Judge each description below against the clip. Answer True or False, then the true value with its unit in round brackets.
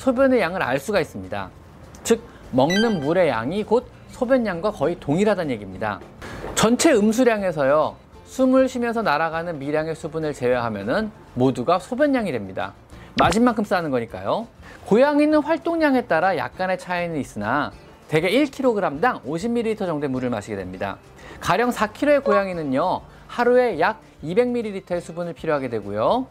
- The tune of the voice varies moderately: False (8.5 semitones)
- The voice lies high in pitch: True (205 Hz)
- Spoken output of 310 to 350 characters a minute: True (335 characters per minute)